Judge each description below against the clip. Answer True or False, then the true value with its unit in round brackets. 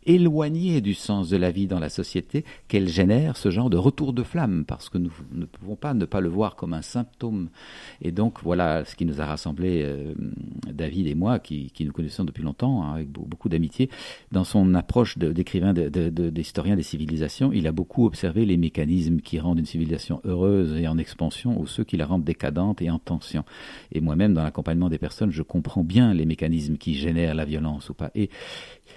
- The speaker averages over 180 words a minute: True (215 wpm)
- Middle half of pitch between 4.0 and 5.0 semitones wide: True (4.3 semitones)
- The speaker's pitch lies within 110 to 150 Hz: False (85 Hz)